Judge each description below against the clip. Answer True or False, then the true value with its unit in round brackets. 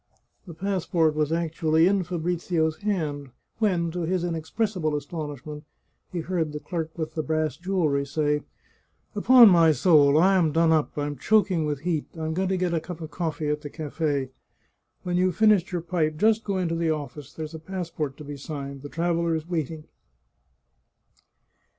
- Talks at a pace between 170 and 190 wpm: True (180 wpm)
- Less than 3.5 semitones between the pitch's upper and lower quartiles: True (2.9 semitones)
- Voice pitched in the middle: True (160 Hz)